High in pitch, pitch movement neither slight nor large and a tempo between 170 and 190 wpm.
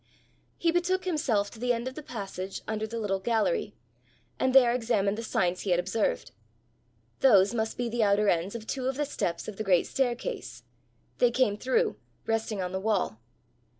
Yes: high, 225 Hz; average, 4.4 semitones; average, 185 wpm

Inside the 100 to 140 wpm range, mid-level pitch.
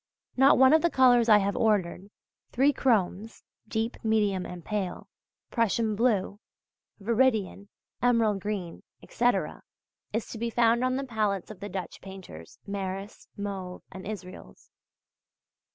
No: slow, 135 wpm; high, 210 Hz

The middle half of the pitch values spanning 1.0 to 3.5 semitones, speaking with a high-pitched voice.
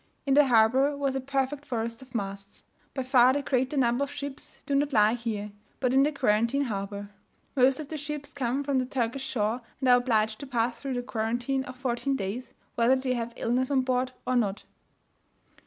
Yes: average, 2.8 semitones; very high, 255 Hz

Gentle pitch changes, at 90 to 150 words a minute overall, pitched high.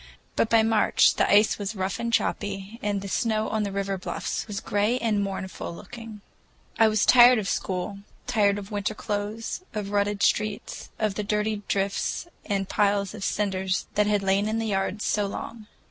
No: narrow, 1.6 semitones; average, 190 wpm; high, 205 Hz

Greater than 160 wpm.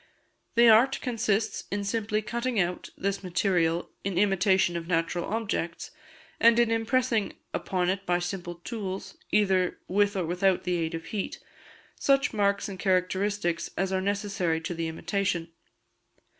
No: average, 145 wpm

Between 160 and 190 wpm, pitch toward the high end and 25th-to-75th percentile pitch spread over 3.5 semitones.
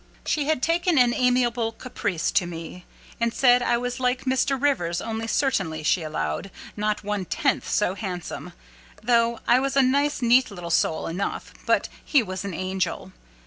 Yes: average, 170 wpm; high, 230 Hz; wide, 5.6 semitones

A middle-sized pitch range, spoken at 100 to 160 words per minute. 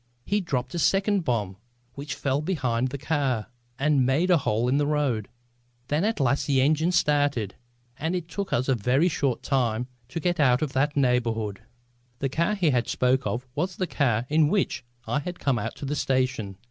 No: average, 4.3 semitones; average, 195 wpm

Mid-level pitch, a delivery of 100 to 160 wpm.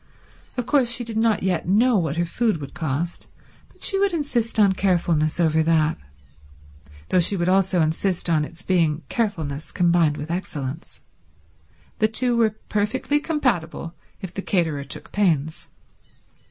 Yes: medium, 180 Hz; average, 155 wpm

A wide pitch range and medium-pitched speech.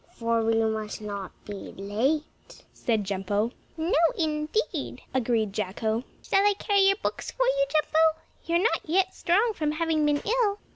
No: wide, 8.0 semitones; very high, 295 Hz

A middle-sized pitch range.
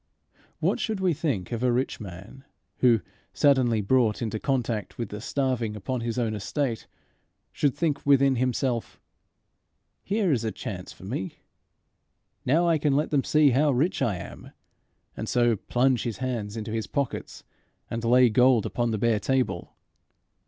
Yes: average, 3.7 semitones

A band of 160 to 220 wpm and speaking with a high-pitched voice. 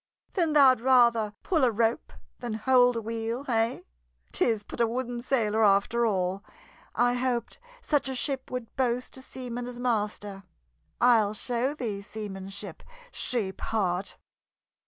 No: average, 140 wpm; high, 235 Hz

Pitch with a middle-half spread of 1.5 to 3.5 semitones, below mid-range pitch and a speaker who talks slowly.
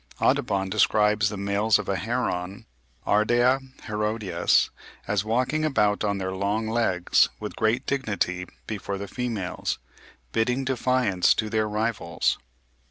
Yes: average, 3.0 semitones; low, 105 Hz; slow, 125 wpm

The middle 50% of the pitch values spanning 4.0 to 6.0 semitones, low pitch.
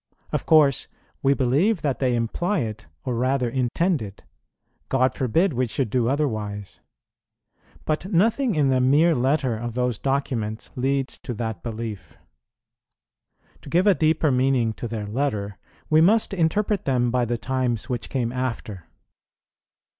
Yes: average, 4.5 semitones; low, 130 Hz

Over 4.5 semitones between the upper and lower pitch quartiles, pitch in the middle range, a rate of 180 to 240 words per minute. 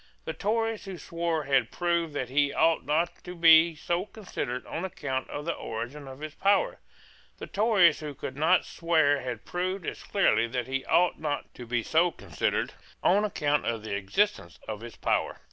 Yes: average, 5.3 semitones; medium, 155 Hz; average, 185 wpm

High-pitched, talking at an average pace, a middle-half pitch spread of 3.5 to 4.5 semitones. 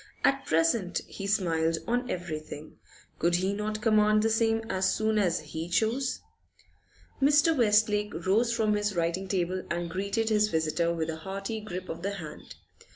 Yes: high, 200 Hz; average, 160 wpm; average, 4.2 semitones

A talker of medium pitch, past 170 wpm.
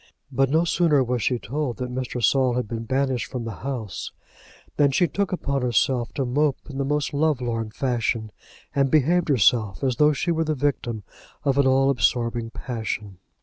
No: low, 130 Hz; average, 190 wpm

